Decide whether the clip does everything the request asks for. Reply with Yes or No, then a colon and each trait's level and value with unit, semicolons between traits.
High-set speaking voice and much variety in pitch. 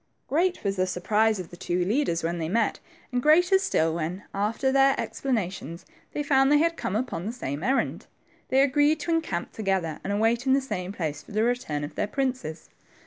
Yes: high, 220 Hz; wide, 7.4 semitones